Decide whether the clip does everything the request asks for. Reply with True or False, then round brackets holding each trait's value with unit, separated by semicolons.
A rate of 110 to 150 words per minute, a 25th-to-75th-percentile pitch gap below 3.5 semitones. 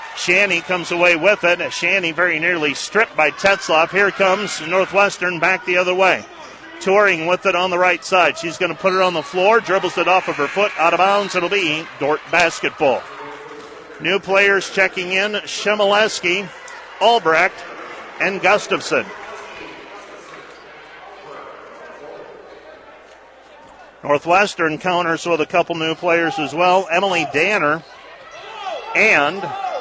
True (135 wpm; 2.7 semitones)